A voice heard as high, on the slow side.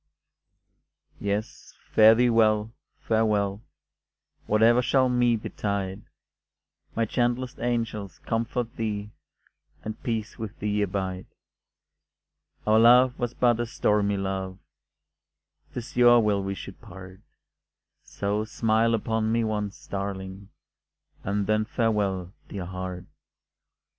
No: low, 110 Hz; slow, 110 wpm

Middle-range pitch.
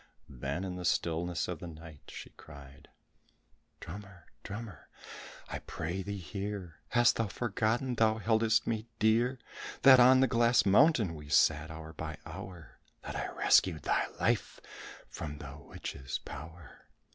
No: very low, 95 Hz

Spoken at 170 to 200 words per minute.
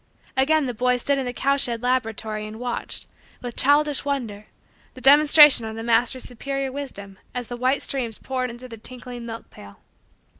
Yes: average, 180 wpm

